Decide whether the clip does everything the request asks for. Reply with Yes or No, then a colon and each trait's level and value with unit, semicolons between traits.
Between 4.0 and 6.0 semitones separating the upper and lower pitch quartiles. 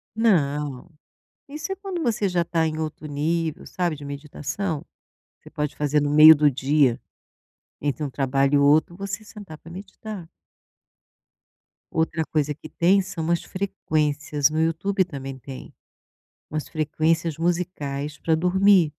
No: average, 3.6 semitones